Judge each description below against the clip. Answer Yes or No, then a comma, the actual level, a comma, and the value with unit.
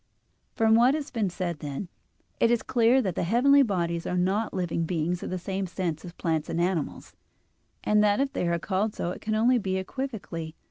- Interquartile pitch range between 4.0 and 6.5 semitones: Yes, average, 4.9 semitones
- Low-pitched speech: No, high, 190 Hz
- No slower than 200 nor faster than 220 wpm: Yes, fast, 205 wpm